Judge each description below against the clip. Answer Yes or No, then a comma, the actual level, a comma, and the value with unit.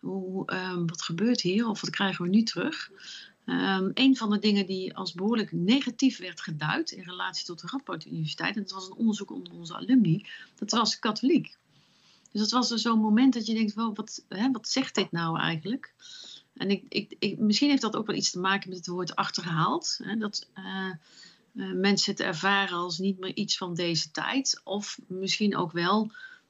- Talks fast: Yes, fast, 205 wpm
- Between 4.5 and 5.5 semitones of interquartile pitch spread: No, average, 3.5 semitones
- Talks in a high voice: Yes, high, 200 Hz